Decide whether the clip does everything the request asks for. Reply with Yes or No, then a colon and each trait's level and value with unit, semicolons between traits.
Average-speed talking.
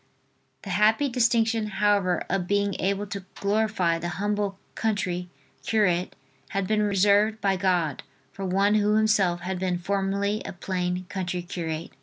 Yes: average, 145 wpm